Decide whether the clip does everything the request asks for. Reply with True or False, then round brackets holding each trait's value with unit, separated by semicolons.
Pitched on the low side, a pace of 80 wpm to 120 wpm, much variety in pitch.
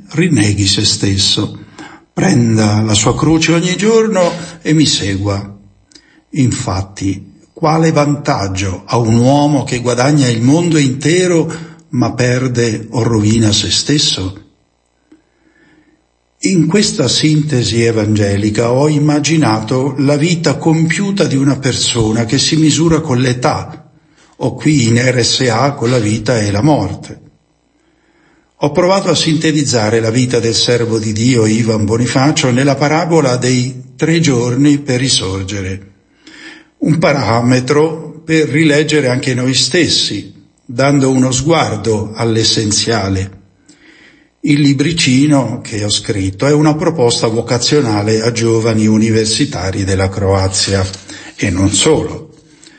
True (125 Hz; 115 wpm; 5.7 semitones)